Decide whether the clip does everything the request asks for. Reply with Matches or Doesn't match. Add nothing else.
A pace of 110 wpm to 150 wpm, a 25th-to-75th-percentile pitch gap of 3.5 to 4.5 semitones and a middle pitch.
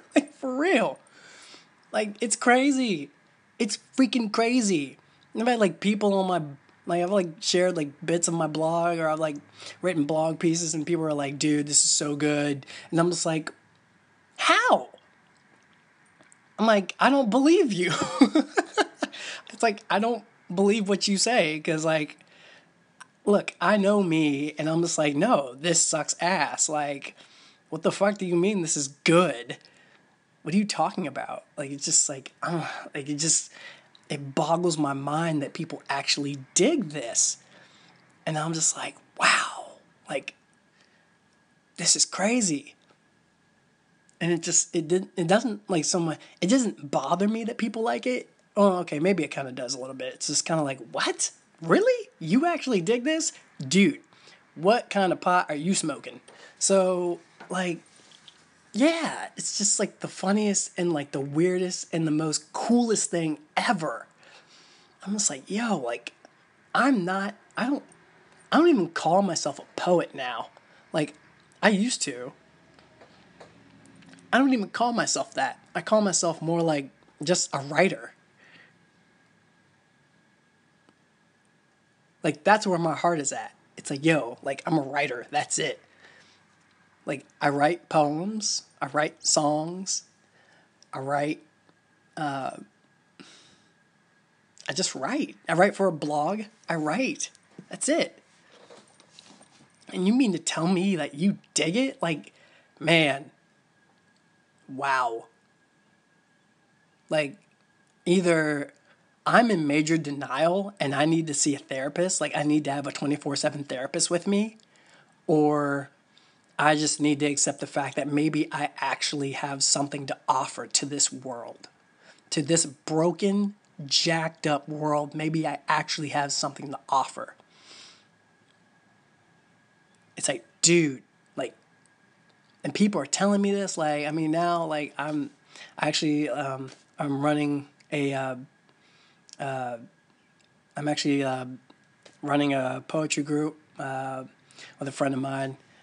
Doesn't match